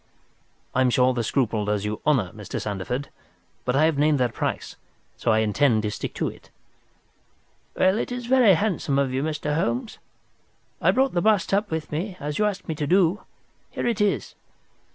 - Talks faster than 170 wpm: Yes, average, 195 wpm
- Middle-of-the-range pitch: Yes, medium, 150 Hz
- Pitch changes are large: Yes, wide, 8.0 semitones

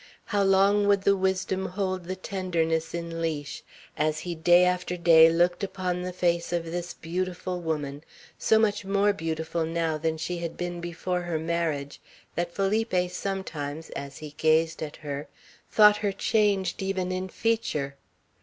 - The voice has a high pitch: No, medium, 175 Hz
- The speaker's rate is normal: Yes, average, 160 wpm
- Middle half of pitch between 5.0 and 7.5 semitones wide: No, average, 2.8 semitones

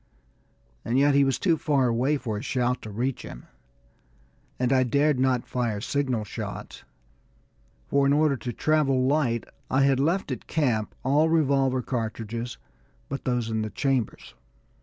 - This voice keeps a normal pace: Yes, average, 160 wpm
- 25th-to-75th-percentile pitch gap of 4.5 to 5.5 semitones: No, average, 2.9 semitones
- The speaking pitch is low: Yes, low, 130 Hz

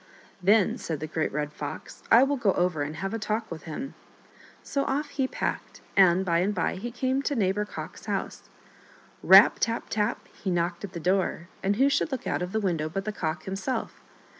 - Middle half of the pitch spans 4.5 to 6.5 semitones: Yes, average, 4.9 semitones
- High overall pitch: Yes, high, 195 Hz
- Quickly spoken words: Yes, fast, 215 wpm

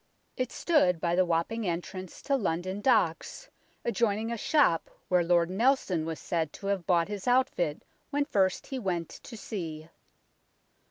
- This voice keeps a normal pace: Yes, average, 155 wpm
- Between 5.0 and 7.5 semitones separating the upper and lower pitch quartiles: Yes, wide, 5.5 semitones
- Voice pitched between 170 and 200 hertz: Yes, medium, 185 Hz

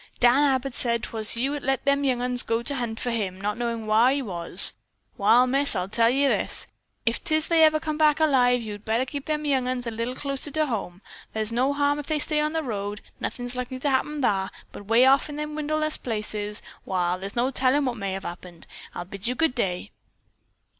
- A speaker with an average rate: No, fast, 225 wpm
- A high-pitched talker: Yes, very high, 250 Hz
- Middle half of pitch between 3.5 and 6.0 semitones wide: Yes, average, 4.7 semitones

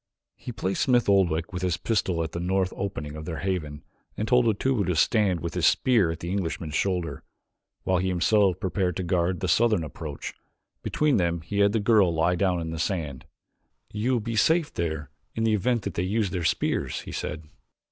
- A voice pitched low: Yes, very low, 95 Hz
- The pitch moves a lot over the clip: No, average, 4.0 semitones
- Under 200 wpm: No, fast, 205 wpm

